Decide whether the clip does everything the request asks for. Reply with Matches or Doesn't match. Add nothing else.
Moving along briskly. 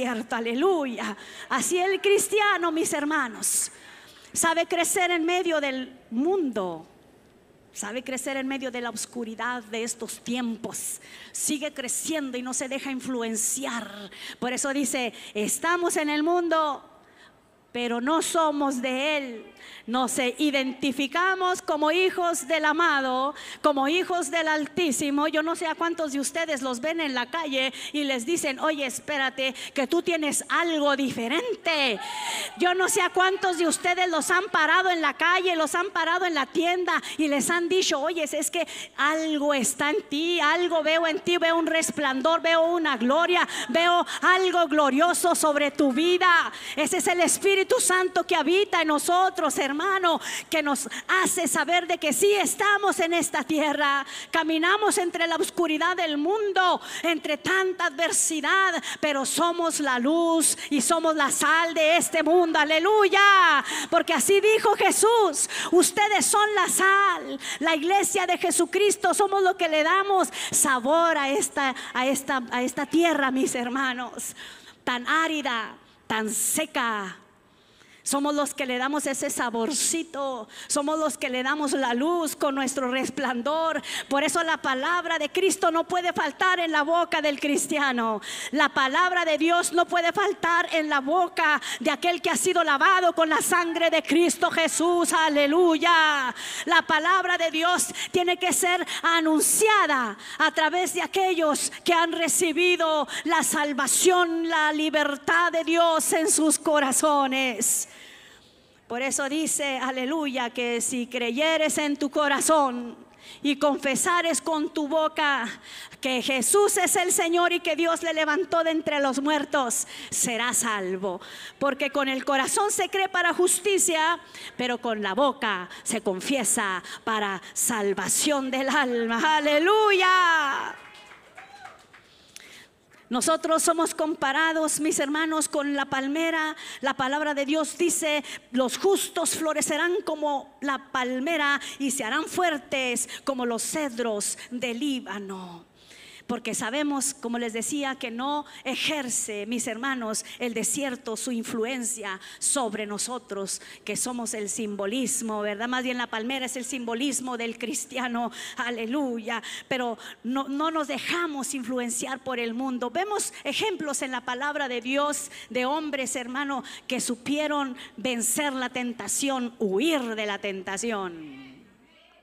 Doesn't match